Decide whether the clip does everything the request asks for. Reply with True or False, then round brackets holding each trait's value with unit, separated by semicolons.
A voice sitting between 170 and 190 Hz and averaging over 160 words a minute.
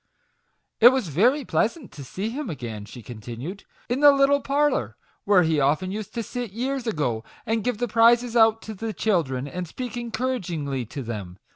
False (210 Hz; 180 wpm)